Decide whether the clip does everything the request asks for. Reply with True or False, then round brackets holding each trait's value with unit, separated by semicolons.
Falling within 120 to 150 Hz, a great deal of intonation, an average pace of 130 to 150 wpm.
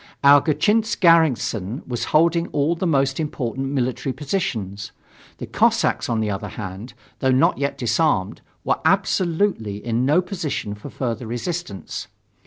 True (135 Hz; 6.4 semitones; 140 wpm)